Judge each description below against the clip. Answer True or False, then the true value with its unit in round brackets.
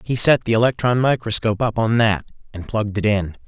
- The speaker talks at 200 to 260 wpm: True (205 wpm)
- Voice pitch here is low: True (110 Hz)